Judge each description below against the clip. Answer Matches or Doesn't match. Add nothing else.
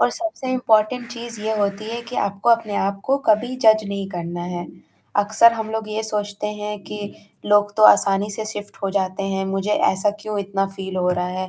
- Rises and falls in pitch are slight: Matches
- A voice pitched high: Matches